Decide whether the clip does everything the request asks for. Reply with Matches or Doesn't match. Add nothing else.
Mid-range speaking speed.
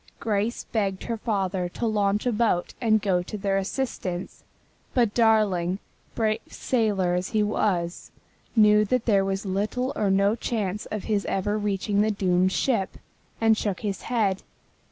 Matches